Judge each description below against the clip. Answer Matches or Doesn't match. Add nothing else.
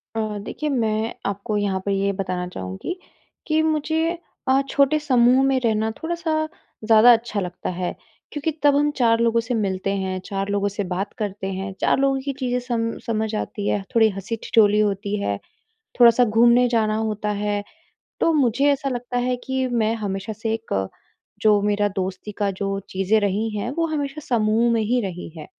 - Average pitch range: Matches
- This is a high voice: Matches